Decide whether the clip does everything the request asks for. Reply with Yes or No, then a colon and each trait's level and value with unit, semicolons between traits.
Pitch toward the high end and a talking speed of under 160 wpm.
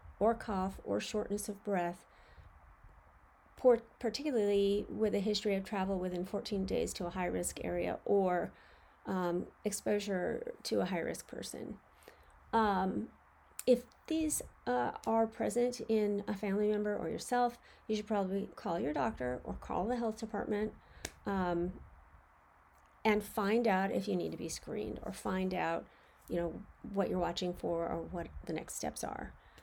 Yes: high, 200 Hz; average, 150 wpm